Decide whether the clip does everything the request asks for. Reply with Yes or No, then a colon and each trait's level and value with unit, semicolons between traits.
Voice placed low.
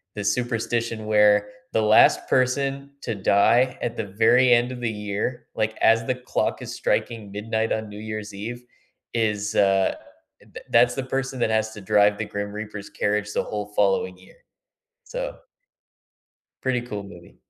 Yes: low, 110 Hz